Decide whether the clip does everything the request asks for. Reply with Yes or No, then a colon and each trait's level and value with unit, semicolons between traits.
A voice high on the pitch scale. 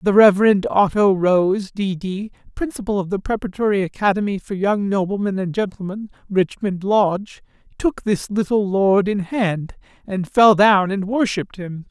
Yes: high, 200 Hz